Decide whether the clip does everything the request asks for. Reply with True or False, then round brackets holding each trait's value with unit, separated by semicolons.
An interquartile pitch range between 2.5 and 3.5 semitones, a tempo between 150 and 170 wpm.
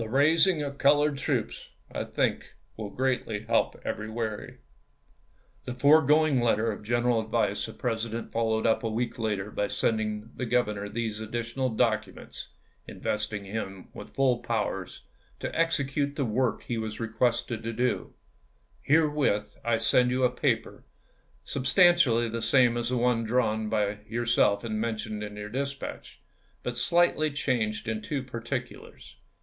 True (3.1 semitones; 155 wpm)